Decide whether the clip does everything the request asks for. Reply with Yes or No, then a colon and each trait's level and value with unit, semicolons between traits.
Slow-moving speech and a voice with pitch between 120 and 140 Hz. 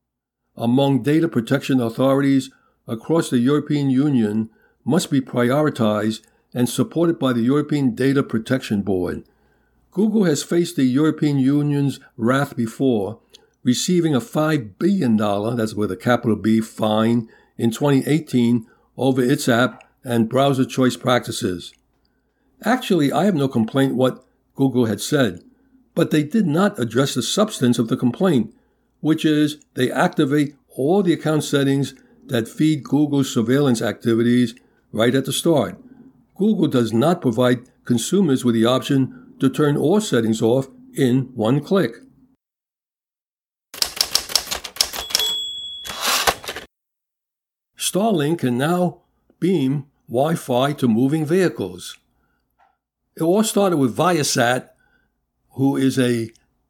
Yes: slow, 125 wpm; low, 135 Hz